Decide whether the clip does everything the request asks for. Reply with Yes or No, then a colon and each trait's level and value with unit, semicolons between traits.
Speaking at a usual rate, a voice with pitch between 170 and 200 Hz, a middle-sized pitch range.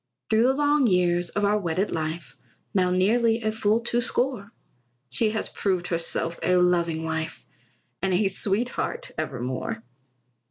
Yes: average, 145 wpm; high, 190 Hz; average, 4.8 semitones